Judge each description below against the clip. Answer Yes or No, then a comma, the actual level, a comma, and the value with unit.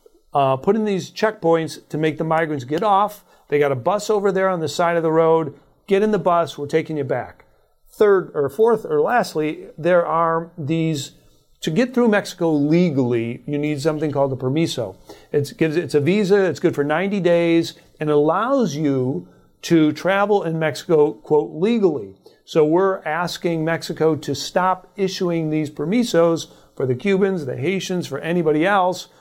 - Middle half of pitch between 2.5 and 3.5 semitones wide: No, average, 4.0 semitones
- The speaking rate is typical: Yes, average, 175 wpm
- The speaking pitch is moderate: Yes, medium, 165 Hz